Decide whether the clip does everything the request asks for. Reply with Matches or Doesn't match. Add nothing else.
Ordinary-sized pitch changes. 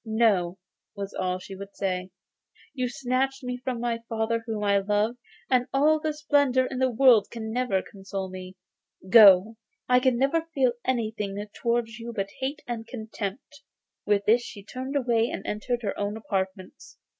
Matches